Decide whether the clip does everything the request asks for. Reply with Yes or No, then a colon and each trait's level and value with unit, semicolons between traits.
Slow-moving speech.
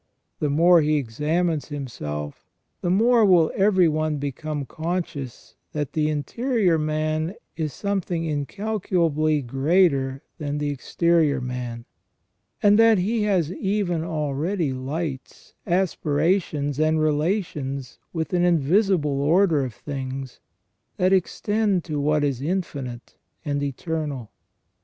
Yes: slow, 115 wpm